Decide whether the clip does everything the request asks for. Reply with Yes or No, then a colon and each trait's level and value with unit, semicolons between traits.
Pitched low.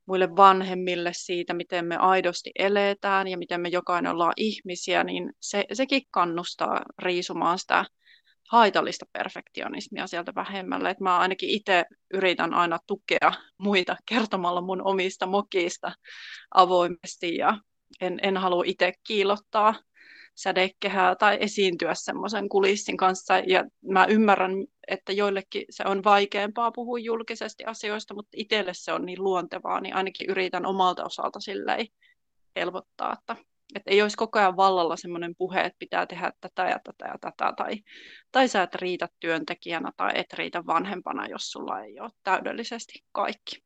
No: high, 190 Hz